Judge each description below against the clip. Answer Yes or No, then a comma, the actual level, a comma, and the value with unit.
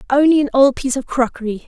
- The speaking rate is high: Yes, fast, 215 wpm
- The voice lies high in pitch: Yes, very high, 260 Hz